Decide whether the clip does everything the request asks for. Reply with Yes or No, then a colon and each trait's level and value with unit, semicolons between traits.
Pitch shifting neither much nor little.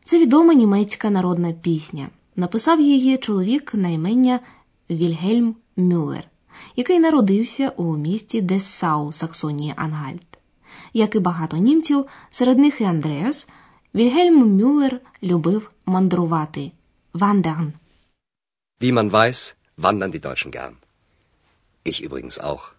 No: wide, 7.3 semitones